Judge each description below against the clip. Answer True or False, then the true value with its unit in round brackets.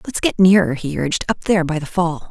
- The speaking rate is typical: False (260 wpm)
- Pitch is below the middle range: False (180 Hz)